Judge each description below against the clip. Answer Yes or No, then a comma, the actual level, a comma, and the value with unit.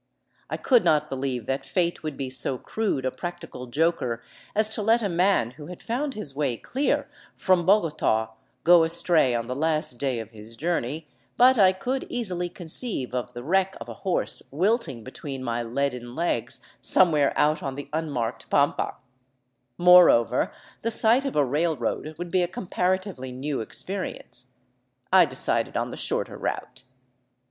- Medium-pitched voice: Yes, medium, 155 Hz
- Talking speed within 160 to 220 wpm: Yes, average, 165 wpm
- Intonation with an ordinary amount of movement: No, wide, 6.4 semitones